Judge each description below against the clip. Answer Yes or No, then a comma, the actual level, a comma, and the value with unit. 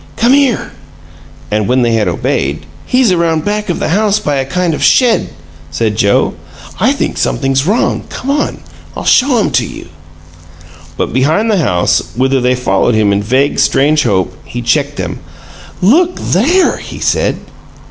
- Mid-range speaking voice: Yes, medium, 145 Hz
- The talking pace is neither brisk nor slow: Yes, average, 170 wpm